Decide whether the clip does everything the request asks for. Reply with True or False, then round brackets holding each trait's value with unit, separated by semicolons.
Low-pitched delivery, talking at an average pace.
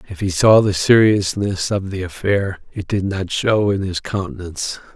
True (95 Hz; 180 wpm)